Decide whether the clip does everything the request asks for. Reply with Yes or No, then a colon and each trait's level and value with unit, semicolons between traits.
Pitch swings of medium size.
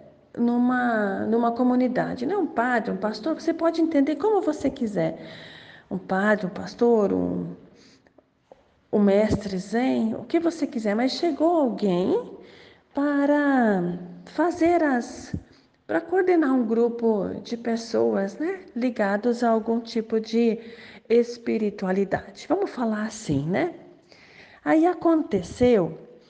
No: wide, 5.8 semitones